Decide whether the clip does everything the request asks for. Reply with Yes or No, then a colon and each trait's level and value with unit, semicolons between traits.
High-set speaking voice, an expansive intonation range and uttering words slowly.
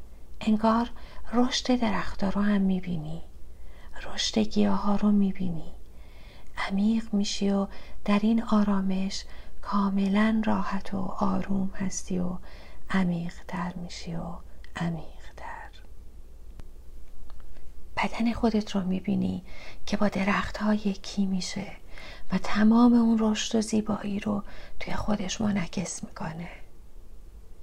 No: high, 195 Hz; average, 3.4 semitones; slow, 110 wpm